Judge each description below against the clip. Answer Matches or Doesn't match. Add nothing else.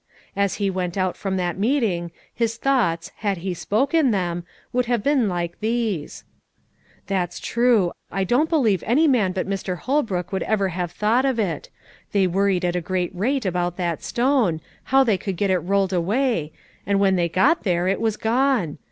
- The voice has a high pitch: Matches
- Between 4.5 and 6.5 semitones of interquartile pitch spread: Matches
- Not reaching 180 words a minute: Doesn't match